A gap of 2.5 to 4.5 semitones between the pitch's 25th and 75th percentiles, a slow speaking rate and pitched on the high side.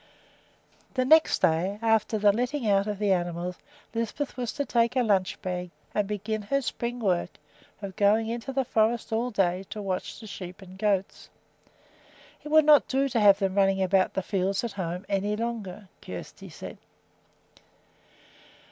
No: average, 3.6 semitones; average, 165 wpm; high, 210 Hz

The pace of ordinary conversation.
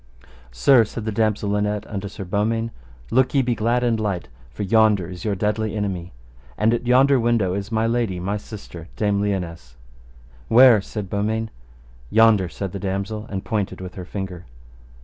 Yes: average, 170 wpm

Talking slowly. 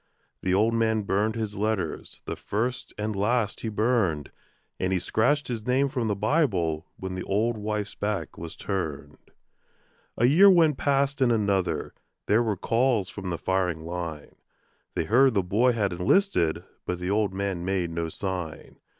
No: average, 165 wpm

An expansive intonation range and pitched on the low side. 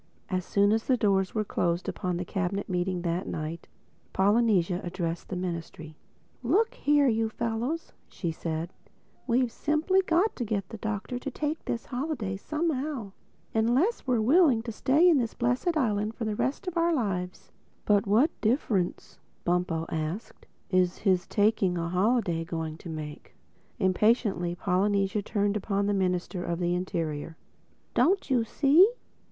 No: wide, 5.9 semitones; high, 205 Hz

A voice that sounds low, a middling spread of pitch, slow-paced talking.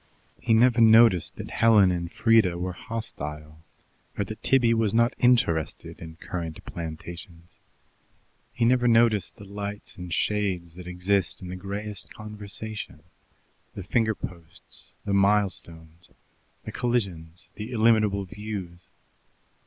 Yes: low, 100 Hz; average, 4.2 semitones; slow, 125 wpm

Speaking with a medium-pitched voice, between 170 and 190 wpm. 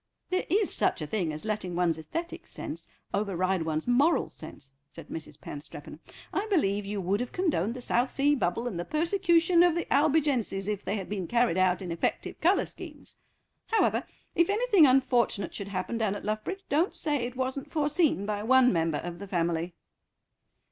No: high, 220 Hz; average, 180 wpm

